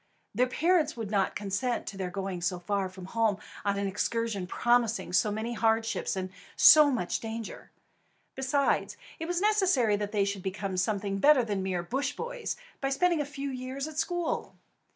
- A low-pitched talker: No, high, 225 Hz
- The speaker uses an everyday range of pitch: No, wide, 5.8 semitones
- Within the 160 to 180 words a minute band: Yes, average, 175 wpm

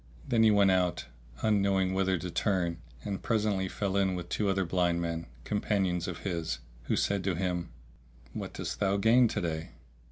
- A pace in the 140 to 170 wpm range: No, average, 180 wpm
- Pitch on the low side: Yes, very low, 95 Hz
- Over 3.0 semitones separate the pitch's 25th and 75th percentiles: No, narrow, 2.5 semitones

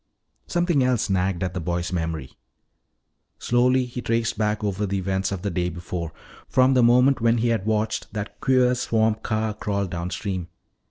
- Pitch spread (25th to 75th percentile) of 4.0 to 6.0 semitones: Yes, average, 4.6 semitones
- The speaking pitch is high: No, low, 105 Hz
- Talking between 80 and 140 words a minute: No, average, 170 wpm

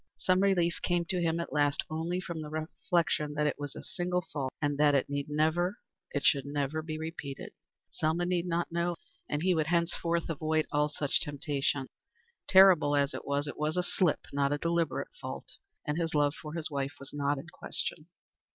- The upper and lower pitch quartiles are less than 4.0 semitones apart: Yes, average, 2.8 semitones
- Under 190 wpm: No, average, 195 wpm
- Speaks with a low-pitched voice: No, medium, 155 Hz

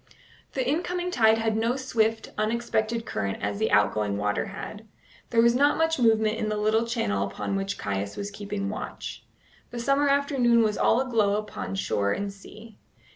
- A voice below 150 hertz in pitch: No, high, 220 Hz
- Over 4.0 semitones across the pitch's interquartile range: No, average, 3.0 semitones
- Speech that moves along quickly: No, average, 175 wpm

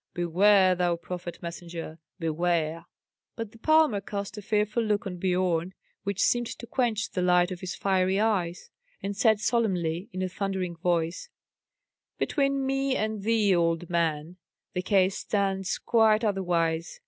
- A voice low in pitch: No, high, 190 Hz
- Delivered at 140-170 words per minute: Yes, average, 150 wpm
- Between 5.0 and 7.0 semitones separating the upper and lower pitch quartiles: No, average, 3.6 semitones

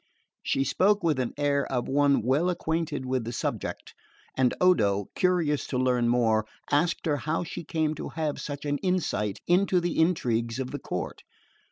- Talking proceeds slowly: No, average, 175 wpm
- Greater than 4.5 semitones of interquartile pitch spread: Yes, average, 5.2 semitones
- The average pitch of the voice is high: No, medium, 145 Hz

